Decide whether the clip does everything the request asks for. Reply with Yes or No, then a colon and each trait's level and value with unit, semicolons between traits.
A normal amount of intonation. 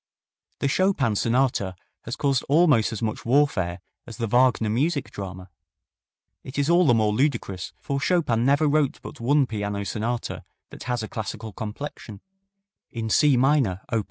Yes: average, 4.7 semitones